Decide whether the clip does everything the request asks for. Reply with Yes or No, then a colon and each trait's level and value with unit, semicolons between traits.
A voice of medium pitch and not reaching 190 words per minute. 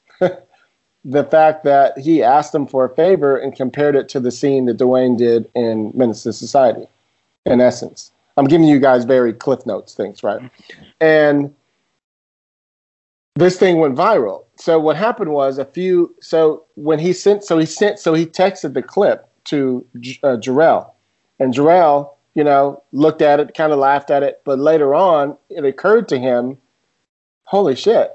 Yes: medium, 145 Hz; average, 165 wpm